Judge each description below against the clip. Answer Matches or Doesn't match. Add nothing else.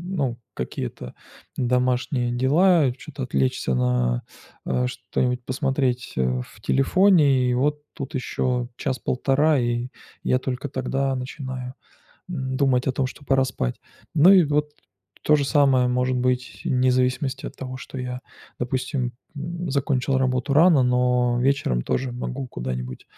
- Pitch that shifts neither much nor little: Doesn't match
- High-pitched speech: Doesn't match